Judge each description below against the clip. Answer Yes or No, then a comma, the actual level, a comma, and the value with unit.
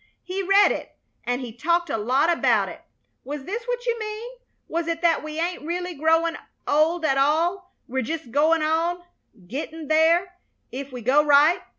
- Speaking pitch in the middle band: No, very high, 325 Hz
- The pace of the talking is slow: No, average, 180 wpm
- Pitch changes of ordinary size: Yes, average, 3.5 semitones